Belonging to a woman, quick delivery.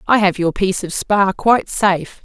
Yes: female; fast, 215 wpm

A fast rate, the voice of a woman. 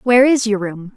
Yes: fast, 250 wpm; female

